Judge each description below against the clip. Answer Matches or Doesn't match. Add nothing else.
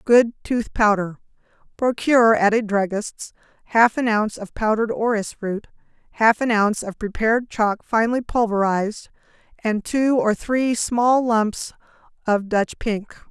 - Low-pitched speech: Doesn't match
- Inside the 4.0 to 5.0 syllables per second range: Matches